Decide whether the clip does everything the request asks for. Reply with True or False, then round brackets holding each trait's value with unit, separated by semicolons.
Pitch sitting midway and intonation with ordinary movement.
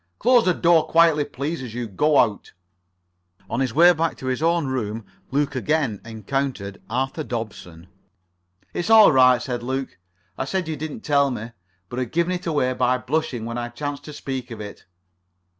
False (130 Hz; 4.7 semitones)